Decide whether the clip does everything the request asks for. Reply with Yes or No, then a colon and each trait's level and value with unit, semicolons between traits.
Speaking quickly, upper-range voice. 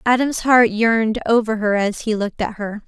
Yes: fast, 210 wpm; high, 220 Hz